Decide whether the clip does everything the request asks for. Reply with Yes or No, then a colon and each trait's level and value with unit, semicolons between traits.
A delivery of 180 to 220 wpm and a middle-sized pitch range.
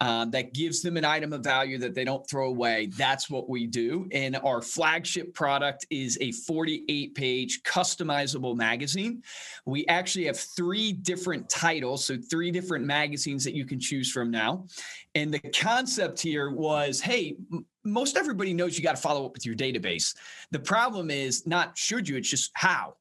Yes: average, 185 wpm; average, 4.8 semitones